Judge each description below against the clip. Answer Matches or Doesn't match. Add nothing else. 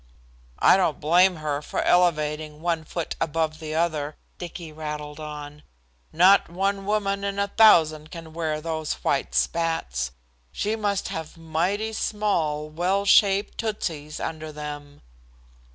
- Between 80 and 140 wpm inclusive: Matches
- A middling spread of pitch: Matches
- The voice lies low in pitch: Doesn't match